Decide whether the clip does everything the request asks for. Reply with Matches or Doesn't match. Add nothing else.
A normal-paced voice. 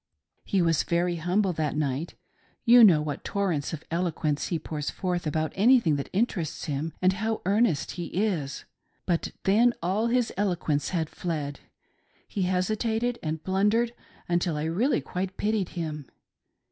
Matches